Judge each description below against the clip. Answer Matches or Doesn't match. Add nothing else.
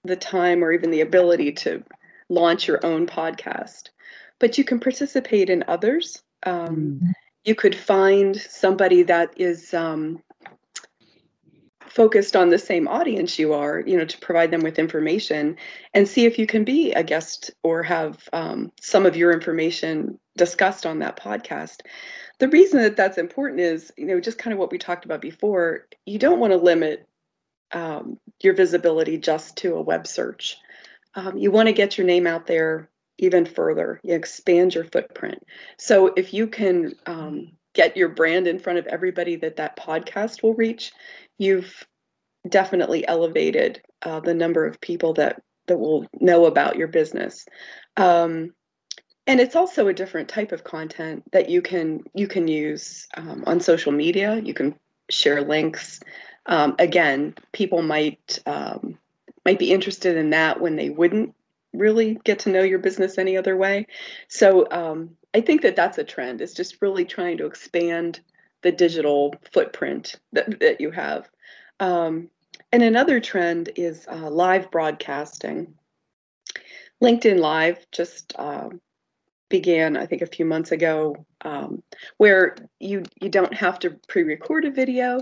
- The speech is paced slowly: Doesn't match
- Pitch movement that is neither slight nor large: Matches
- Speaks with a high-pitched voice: Doesn't match